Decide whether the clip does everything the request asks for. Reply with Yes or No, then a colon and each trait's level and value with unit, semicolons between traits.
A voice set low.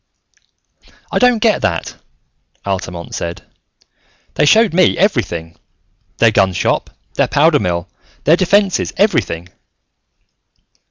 Yes: low, 125 Hz